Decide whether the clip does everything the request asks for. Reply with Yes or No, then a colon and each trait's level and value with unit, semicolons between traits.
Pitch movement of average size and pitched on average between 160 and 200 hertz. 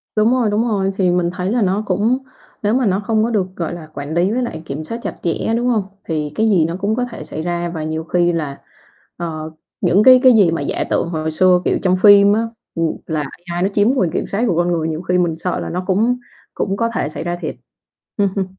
Yes: average, 4.3 semitones; medium, 185 Hz